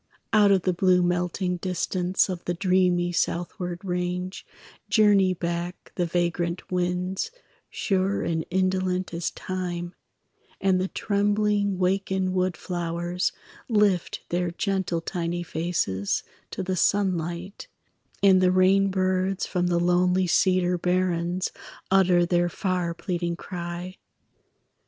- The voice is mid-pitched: Yes, medium, 180 Hz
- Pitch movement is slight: Yes, narrow, 1.3 semitones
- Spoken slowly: Yes, slow, 115 wpm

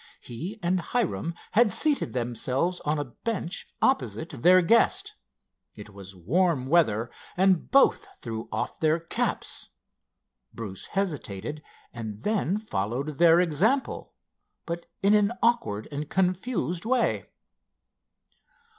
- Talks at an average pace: No, slow, 115 wpm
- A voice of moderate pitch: Yes, medium, 170 Hz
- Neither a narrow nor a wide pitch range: No, wide, 8.3 semitones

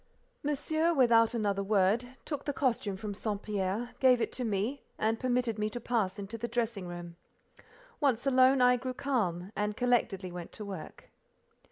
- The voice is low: No, high, 230 Hz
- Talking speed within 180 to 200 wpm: No, average, 170 wpm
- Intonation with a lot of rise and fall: No, average, 4.1 semitones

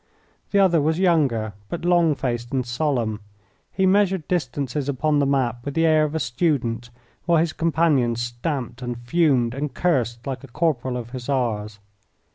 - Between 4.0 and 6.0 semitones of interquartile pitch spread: Yes, average, 5.2 semitones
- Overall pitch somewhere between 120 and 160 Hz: Yes, medium, 140 Hz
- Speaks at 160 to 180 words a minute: Yes, average, 165 wpm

